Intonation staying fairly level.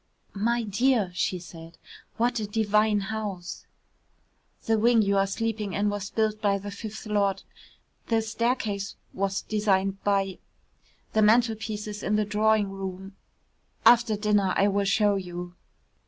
Yes: narrow, 1.9 semitones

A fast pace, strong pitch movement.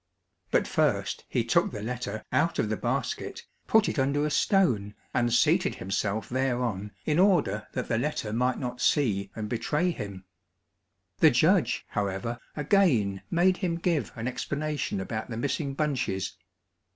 No: average, 150 wpm; wide, 6.1 semitones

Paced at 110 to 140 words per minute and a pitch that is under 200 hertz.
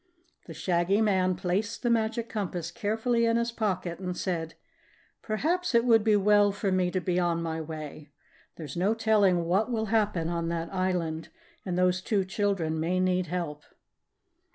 No: average, 170 wpm; medium, 185 Hz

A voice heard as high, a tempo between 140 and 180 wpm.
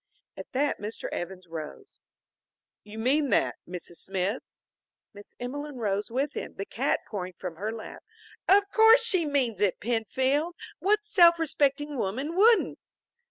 Yes: very high, 260 Hz; average, 145 wpm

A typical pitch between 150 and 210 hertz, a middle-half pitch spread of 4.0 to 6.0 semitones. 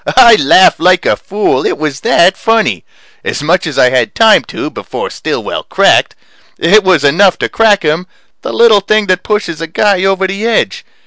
Yes: high, 190 Hz; average, 4.5 semitones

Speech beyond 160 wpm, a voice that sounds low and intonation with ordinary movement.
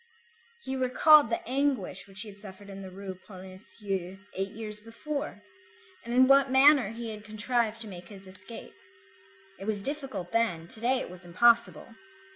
No: average, 170 wpm; high, 215 Hz; average, 4.4 semitones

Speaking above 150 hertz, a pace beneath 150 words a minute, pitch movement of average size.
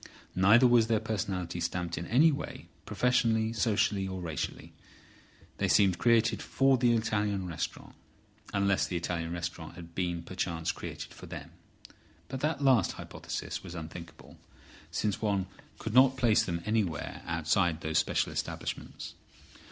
No: low, 100 Hz; average, 140 wpm; average, 5.0 semitones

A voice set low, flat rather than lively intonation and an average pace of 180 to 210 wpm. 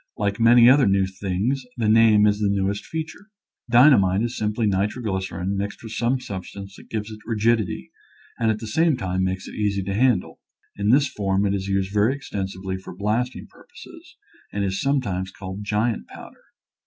No: low, 105 Hz; average, 3.2 semitones; average, 185 wpm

